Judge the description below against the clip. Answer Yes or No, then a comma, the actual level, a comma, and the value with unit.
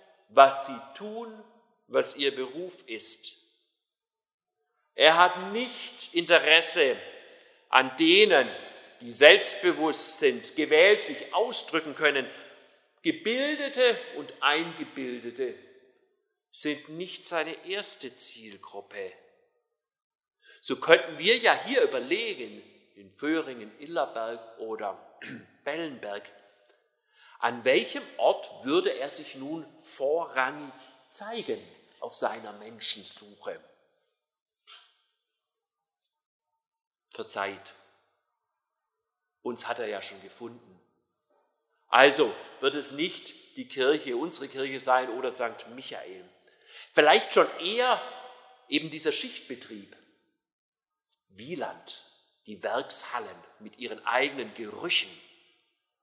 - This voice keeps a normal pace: No, slow, 90 wpm